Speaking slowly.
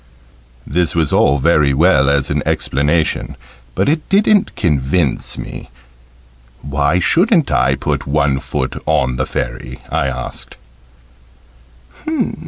Yes: slow, 115 wpm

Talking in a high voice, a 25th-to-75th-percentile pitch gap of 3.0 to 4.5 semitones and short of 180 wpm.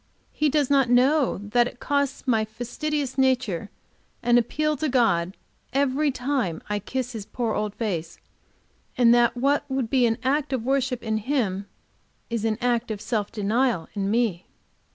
Yes: high, 245 Hz; average, 3.7 semitones; average, 165 wpm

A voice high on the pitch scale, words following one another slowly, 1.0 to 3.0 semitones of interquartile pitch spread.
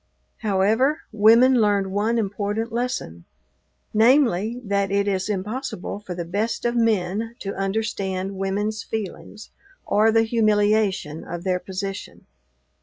Yes: high, 205 Hz; slow, 120 wpm; average, 2.7 semitones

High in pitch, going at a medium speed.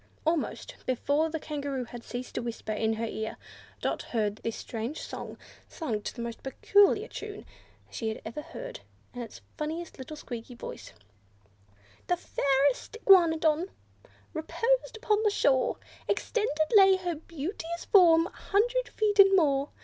Yes: very high, 315 Hz; average, 155 wpm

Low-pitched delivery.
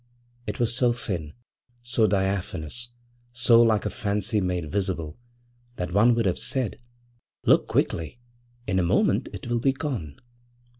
Yes: low, 105 Hz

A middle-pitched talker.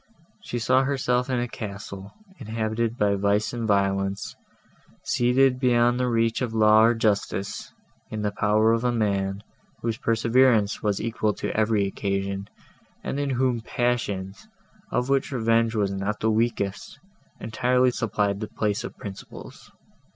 No: low, 110 Hz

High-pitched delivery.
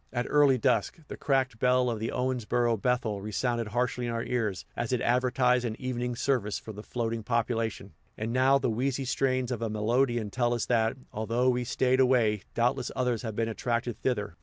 No: low, 120 Hz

